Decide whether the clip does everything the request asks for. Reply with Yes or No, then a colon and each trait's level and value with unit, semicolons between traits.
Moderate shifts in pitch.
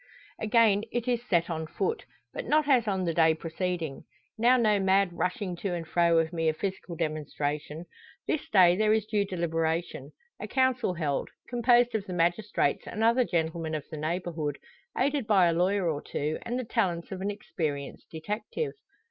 Yes: average, 5.0 semitones